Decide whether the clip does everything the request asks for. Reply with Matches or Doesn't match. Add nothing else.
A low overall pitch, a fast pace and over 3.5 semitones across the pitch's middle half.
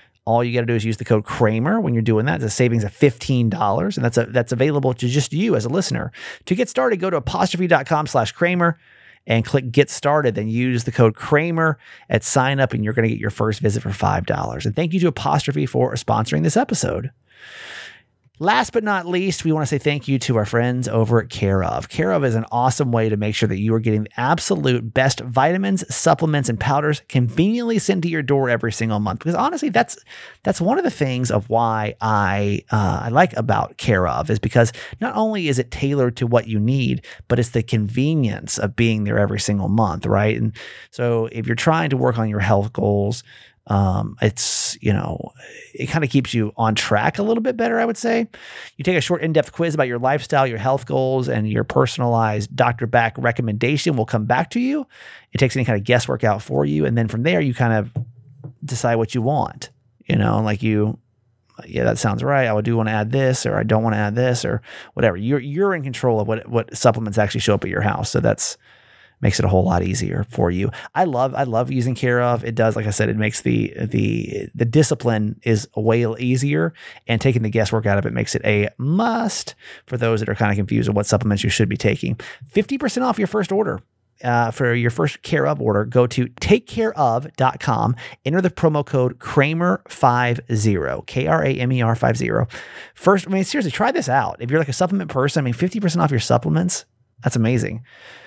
Matches